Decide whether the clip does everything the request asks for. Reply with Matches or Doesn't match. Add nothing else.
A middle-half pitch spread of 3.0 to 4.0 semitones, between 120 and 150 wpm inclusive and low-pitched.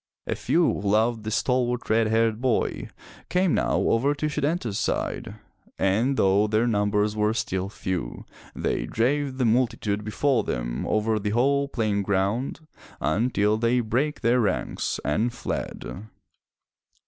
Matches